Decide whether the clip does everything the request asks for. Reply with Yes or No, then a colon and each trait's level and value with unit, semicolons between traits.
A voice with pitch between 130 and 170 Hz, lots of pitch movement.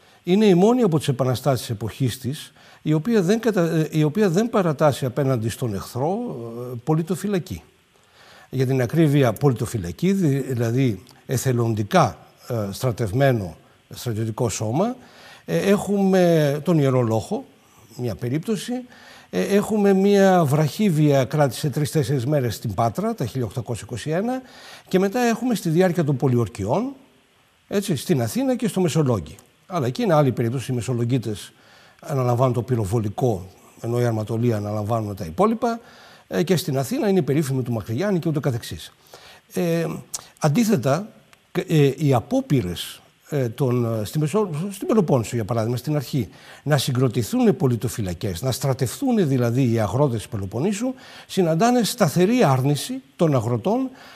Yes: medium, 140 Hz; wide, 7.5 semitones